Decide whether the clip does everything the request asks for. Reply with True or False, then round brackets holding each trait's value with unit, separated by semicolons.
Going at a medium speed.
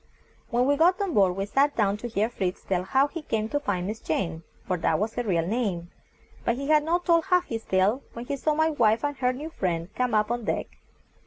False (245 wpm)